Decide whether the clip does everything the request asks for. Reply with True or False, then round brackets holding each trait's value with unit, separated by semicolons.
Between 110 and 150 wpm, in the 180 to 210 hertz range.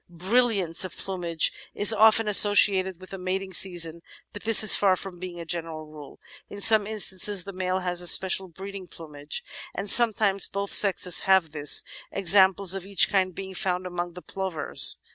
False (175 wpm; 190 Hz)